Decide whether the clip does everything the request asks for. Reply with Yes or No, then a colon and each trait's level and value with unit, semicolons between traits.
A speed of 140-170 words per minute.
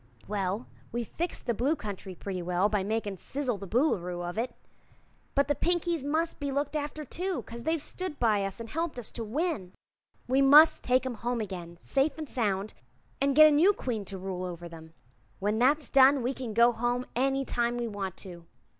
No: average, 200 wpm